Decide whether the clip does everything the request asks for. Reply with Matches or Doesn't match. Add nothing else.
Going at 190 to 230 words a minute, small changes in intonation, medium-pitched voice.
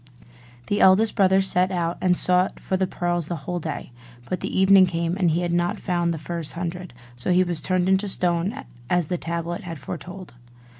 Matches